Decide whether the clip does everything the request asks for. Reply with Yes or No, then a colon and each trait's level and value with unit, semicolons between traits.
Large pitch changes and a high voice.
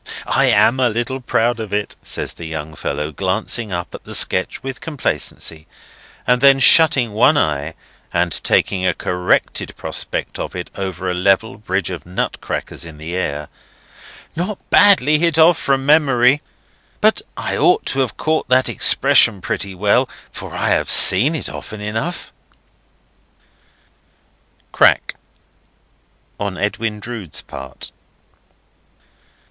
No: wide, 6.8 semitones; low, 110 Hz